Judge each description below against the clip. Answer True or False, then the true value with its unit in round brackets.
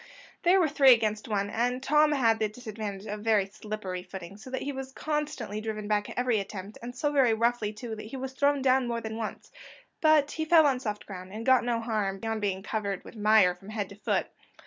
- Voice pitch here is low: False (220 Hz)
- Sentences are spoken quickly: True (230 wpm)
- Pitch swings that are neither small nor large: True (3.9 semitones)